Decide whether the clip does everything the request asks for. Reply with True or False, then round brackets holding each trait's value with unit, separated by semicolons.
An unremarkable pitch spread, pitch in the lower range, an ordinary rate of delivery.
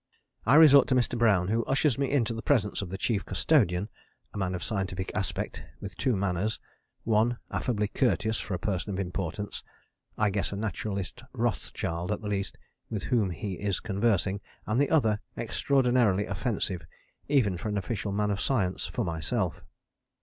True (3.4 semitones; 105 Hz; 170 wpm)